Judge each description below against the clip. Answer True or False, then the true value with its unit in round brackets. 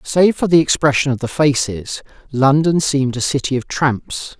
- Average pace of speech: True (175 wpm)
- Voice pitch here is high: False (140 Hz)